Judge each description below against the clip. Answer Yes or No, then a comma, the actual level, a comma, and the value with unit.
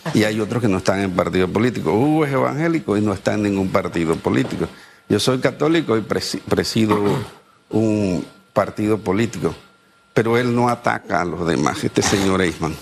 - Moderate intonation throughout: Yes, average, 3.8 semitones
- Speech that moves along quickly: No, average, 180 wpm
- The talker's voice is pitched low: Yes, low, 105 Hz